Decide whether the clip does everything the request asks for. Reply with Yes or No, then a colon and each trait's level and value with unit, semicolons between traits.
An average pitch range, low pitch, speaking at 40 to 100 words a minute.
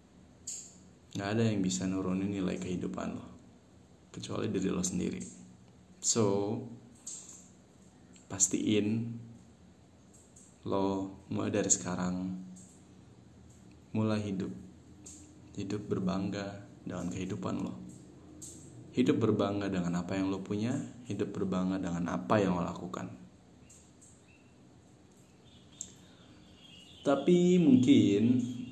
Yes: average, 3.9 semitones; very low, 95 Hz; slow, 85 wpm